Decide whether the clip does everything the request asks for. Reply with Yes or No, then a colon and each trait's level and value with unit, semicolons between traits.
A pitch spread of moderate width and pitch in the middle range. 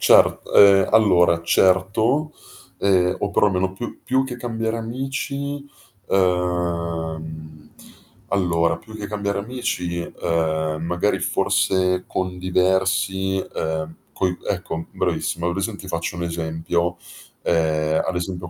No: average, 3.2 semitones; very low, 90 Hz